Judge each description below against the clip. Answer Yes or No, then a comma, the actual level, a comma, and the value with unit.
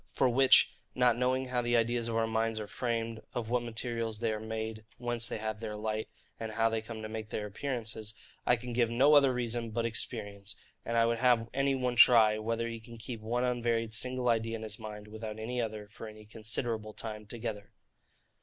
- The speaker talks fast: Yes, fast, 210 wpm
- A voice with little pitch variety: Yes, narrow, 1.7 semitones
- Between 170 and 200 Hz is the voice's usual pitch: No, low, 115 Hz